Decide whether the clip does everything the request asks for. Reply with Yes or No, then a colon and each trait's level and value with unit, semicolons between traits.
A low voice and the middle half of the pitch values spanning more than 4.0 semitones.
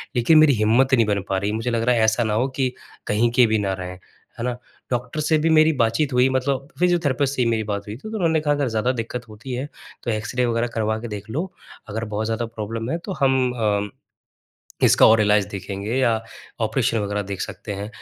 No: low, 115 Hz; average, 3.7 semitones